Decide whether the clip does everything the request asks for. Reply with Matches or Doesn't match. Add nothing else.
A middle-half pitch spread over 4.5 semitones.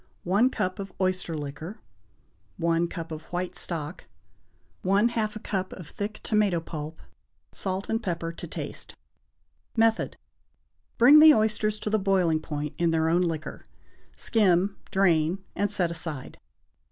Doesn't match